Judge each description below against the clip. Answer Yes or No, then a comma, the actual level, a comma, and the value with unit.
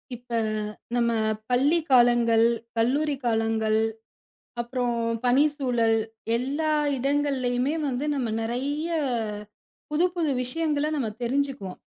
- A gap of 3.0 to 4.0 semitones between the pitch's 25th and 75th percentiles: Yes, average, 3.5 semitones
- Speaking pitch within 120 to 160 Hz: No, very high, 250 Hz